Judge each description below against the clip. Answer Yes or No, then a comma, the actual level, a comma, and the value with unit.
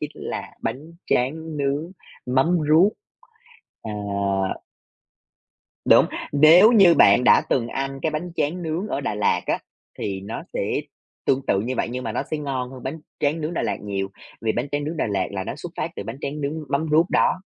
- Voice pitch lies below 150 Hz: Yes, medium, 140 Hz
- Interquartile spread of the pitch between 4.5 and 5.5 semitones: Yes, average, 4.8 semitones